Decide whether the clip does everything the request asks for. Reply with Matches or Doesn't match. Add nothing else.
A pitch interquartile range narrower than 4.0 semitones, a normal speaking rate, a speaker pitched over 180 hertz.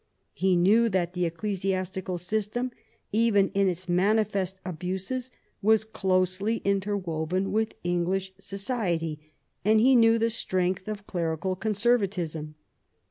Doesn't match